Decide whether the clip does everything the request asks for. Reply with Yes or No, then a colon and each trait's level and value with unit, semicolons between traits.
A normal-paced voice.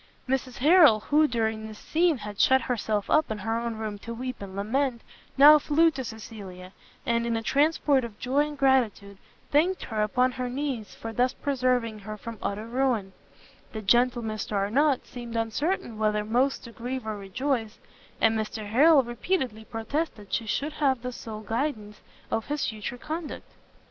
Yes: average, 175 wpm